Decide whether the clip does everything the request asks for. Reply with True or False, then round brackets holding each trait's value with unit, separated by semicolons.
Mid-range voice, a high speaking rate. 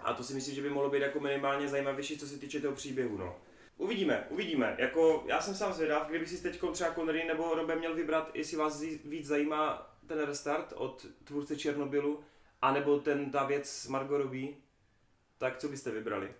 True (145 Hz; 190 wpm)